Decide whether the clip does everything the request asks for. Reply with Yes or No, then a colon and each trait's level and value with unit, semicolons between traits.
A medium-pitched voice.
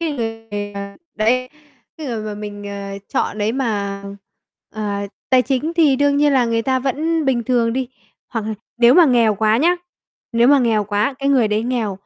No: high, 235 Hz